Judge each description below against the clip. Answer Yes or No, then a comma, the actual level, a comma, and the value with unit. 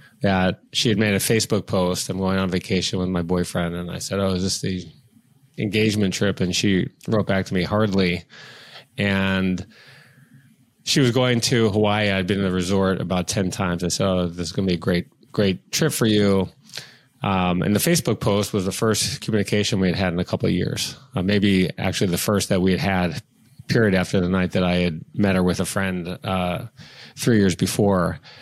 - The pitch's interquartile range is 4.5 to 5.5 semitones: No, average, 2.8 semitones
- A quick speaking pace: Yes, fast, 210 wpm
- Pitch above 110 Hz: No, very low, 95 Hz